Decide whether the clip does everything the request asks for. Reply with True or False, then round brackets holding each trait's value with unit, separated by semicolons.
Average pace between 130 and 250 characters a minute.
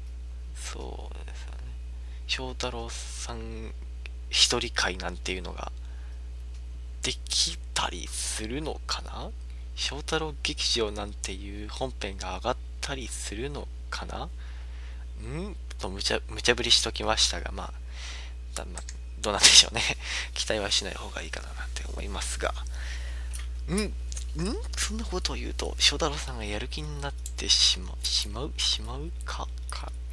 False (275 characters per minute)